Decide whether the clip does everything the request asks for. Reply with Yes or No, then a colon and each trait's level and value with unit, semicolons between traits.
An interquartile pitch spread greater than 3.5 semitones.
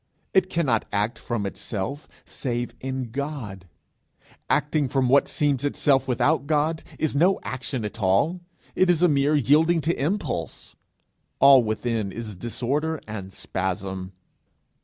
Yes: wide, 5.6 semitones